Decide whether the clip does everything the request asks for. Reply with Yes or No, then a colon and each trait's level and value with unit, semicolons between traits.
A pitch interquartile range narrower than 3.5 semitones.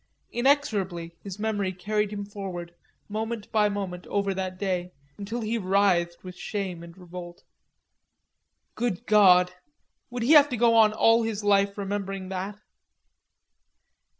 Yes: average, 2.9 semitones